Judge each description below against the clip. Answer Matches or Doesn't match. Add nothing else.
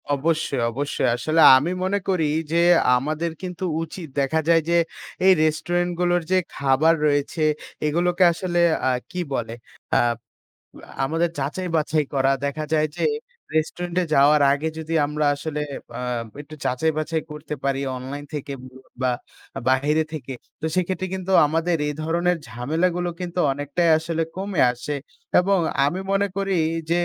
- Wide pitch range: Doesn't match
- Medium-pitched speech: Matches